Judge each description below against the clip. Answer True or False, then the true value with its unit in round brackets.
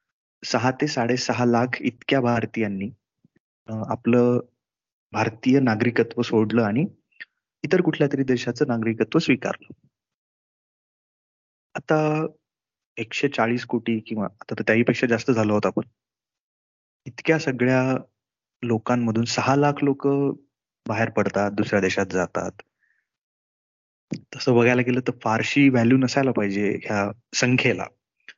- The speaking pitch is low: True (120 Hz)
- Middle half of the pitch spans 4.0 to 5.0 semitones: False (3.3 semitones)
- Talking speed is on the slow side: False (110 wpm)